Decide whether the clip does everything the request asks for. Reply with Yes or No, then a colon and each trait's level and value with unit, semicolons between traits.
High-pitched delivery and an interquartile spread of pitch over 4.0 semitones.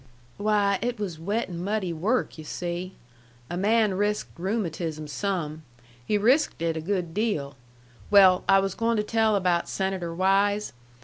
No: high, 195 Hz; average, 3.5 semitones